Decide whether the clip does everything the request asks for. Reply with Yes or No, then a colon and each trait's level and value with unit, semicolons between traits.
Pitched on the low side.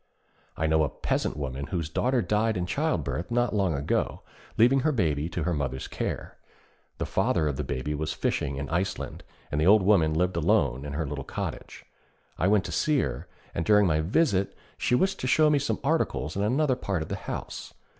Yes: very low, 90 Hz